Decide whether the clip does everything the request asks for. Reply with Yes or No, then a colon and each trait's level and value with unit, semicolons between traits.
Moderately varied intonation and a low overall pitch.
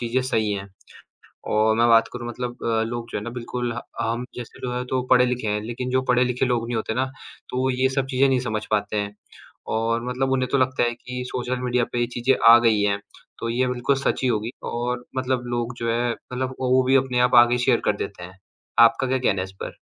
No: narrow, 1.8 semitones; low, 120 Hz